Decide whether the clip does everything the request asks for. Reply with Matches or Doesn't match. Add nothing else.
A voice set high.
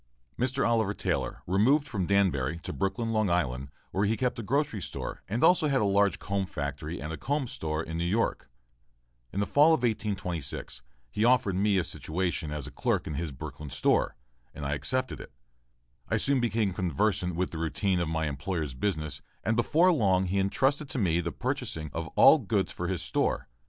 Doesn't match